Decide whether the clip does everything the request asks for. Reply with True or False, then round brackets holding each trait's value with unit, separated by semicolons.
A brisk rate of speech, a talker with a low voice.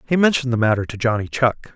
True (240 wpm; 125 Hz)